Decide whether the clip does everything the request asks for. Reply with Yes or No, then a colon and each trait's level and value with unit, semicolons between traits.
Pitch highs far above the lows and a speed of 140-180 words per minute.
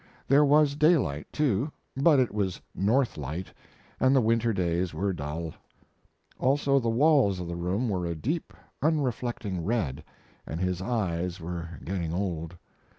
Yes: wide, 7.4 semitones; average, 150 wpm